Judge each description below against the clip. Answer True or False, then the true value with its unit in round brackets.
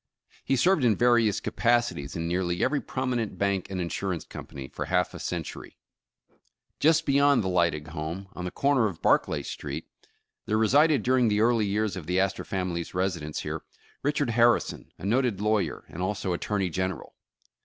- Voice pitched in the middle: False (100 Hz)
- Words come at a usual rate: True (170 wpm)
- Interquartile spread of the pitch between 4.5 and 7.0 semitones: True (5.2 semitones)